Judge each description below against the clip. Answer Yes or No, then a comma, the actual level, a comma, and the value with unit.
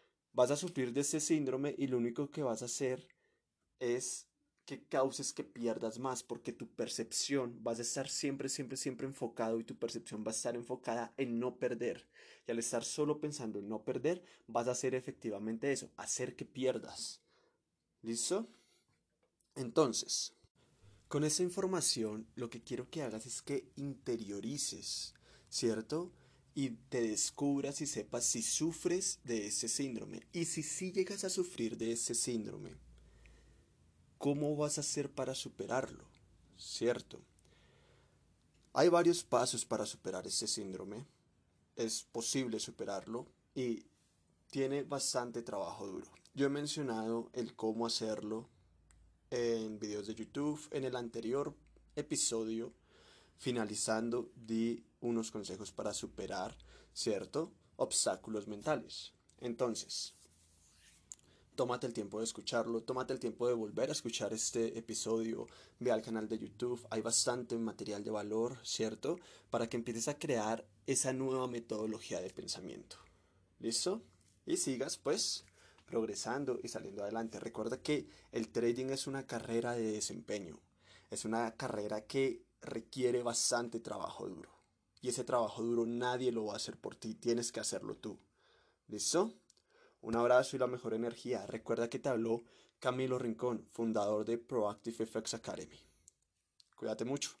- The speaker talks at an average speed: Yes, average, 140 wpm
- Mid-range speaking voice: No, low, 120 Hz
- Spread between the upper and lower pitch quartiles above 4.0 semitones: No, average, 2.9 semitones